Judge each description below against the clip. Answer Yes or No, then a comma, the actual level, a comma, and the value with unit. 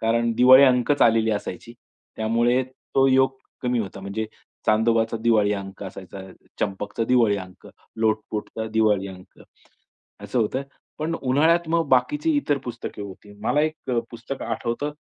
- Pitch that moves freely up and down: No, average, 3.9 semitones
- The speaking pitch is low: Yes, low, 115 Hz